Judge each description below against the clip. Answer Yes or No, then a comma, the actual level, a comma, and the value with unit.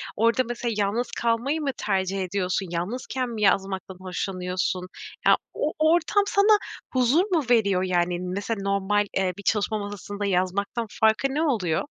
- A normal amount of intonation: Yes, average, 4.4 semitones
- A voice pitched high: Yes, high, 205 Hz